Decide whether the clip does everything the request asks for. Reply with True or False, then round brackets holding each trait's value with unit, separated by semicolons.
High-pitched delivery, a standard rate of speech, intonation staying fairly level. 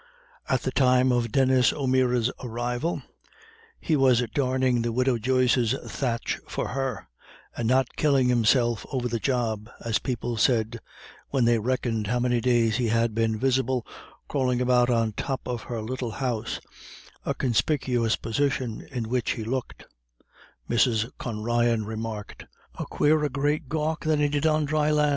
False (125 Hz; 155 wpm; 2.3 semitones)